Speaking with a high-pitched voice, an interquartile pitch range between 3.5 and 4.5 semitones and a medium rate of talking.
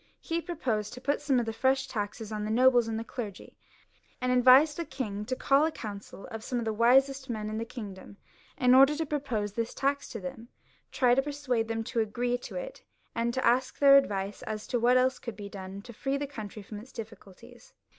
No: high, 245 Hz; average, 3.8 semitones; fast, 215 wpm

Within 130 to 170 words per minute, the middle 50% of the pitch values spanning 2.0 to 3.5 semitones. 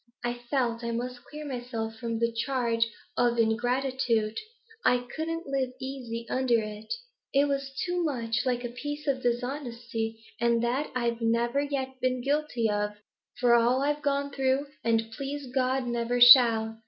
Yes: average, 160 wpm; narrow, 2.6 semitones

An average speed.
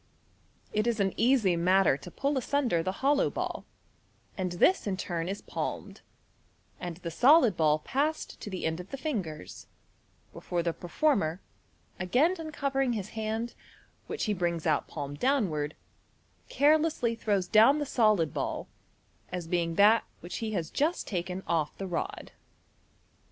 Yes: average, 150 wpm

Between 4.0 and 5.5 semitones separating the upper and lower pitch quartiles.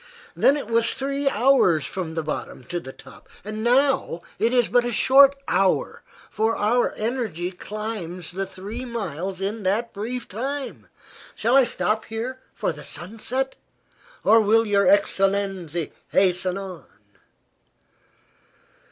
Yes: average, 4.7 semitones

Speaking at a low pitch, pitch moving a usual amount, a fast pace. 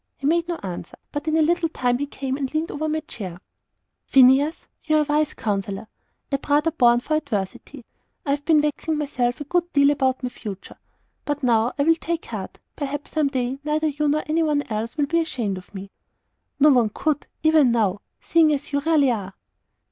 No: very high, 285 Hz; average, 4.1 semitones; fast, 210 wpm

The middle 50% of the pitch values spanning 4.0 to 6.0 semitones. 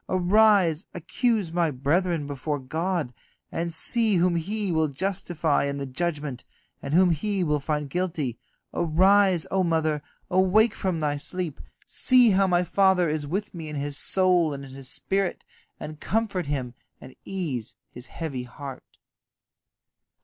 Yes: average, 4.5 semitones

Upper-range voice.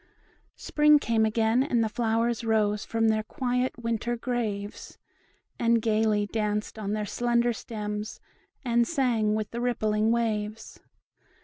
Yes: high, 225 Hz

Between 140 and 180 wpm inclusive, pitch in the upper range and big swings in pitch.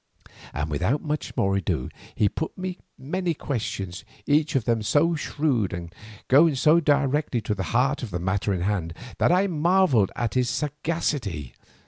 No: average, 160 wpm; low, 130 Hz; wide, 7.7 semitones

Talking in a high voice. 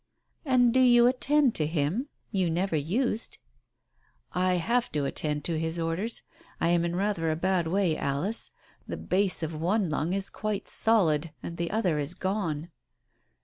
No: medium, 180 Hz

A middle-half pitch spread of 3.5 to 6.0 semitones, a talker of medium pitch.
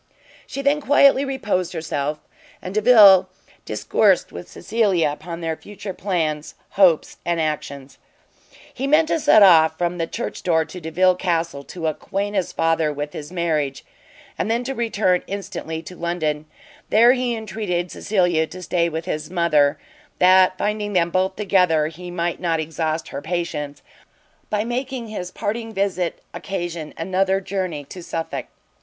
Yes: average, 4.0 semitones; medium, 180 Hz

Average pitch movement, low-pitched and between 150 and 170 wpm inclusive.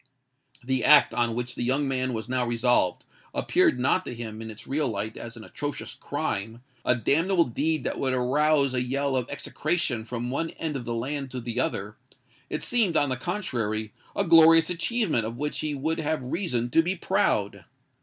No: average, 4.5 semitones; low, 130 Hz; average, 185 wpm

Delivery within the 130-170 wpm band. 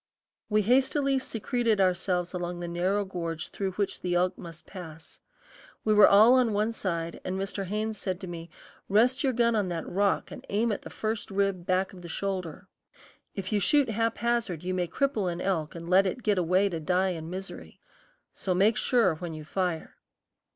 No: average, 195 wpm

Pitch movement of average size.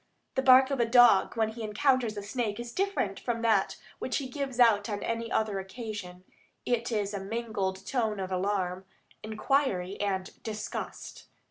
Yes: average, 3.4 semitones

